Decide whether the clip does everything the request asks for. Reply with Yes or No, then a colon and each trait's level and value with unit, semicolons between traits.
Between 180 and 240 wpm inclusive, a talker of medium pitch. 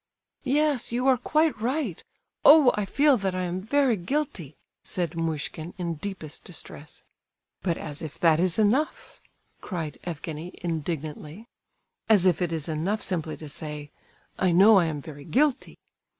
No: average, 150 wpm; medium, 180 Hz